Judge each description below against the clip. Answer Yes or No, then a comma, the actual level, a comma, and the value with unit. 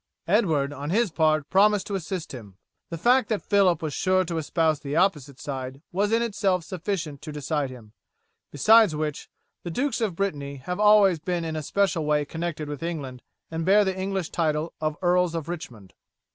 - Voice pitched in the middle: Yes, medium, 165 Hz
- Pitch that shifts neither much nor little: Yes, average, 4.5 semitones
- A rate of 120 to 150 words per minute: No, average, 185 wpm